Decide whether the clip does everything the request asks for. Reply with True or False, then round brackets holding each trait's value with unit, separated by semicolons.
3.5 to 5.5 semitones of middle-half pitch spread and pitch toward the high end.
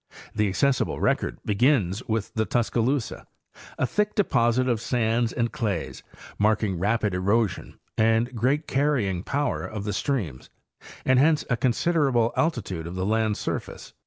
False (3.9 semitones; 115 Hz)